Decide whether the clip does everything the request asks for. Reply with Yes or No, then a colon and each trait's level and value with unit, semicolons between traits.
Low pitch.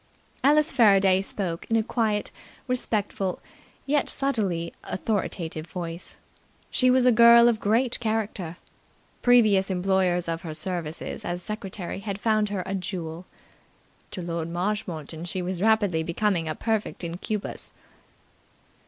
No: high, 195 Hz